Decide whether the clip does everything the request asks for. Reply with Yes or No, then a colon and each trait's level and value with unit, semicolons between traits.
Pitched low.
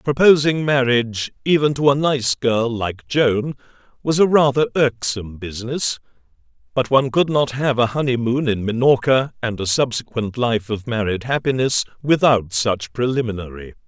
Yes: low, 125 Hz